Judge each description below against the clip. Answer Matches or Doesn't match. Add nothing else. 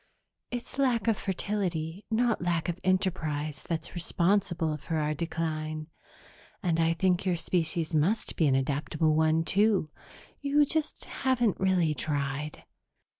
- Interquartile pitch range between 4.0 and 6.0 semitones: Matches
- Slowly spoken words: Matches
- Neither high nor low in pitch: Matches